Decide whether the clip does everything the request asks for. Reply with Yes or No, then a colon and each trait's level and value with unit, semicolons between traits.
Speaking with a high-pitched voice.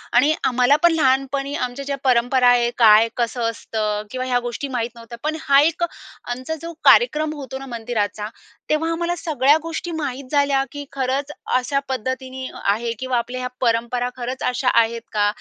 Yes: very high, 255 Hz